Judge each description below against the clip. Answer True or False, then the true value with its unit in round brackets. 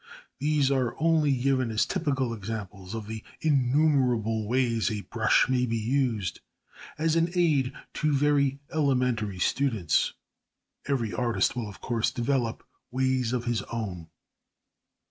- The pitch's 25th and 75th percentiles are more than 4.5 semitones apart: False (3.9 semitones)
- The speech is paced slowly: True (130 wpm)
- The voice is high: False (125 Hz)